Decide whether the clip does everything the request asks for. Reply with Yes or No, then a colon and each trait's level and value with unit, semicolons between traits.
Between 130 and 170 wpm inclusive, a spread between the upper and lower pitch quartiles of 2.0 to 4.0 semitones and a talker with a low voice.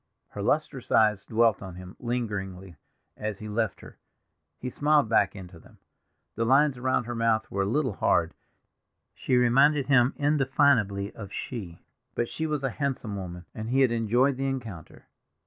No: average, 165 wpm; average, 4.9 semitones; low, 115 Hz